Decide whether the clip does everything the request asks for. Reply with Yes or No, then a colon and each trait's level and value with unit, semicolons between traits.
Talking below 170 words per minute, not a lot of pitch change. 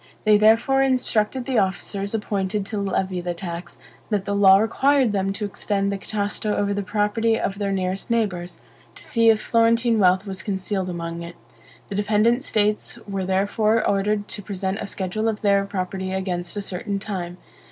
No: average, 175 wpm; narrow, 2.2 semitones